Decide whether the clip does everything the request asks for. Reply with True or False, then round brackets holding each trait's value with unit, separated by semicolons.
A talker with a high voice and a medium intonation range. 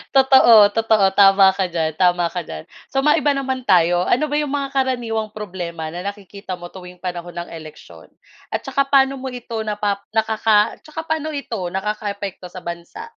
False (205 Hz; 6.7 semitones)